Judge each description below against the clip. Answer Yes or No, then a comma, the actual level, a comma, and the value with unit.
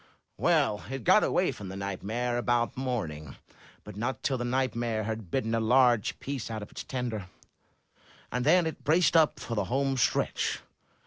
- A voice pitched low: Yes, low, 120 Hz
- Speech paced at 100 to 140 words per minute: No, average, 175 wpm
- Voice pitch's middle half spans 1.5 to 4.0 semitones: Yes, average, 3.5 semitones